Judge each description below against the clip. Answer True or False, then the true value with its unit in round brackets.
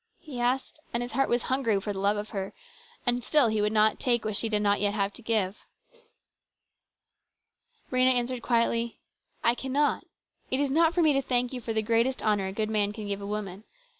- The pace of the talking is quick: True (220 wpm)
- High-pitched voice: True (230 Hz)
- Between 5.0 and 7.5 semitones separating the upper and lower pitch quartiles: False (3.5 semitones)